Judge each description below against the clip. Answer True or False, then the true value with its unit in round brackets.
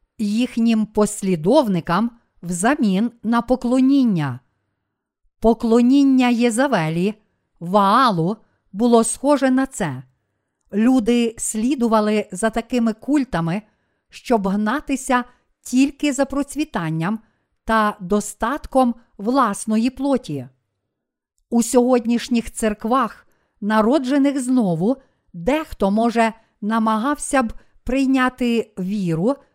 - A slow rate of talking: True (75 wpm)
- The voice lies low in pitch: False (230 Hz)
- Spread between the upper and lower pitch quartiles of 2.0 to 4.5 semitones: True (4.1 semitones)